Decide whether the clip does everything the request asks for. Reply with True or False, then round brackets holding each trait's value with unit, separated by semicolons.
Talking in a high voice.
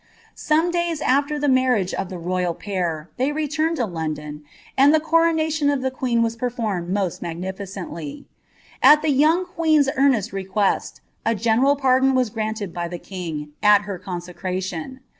True (225 Hz)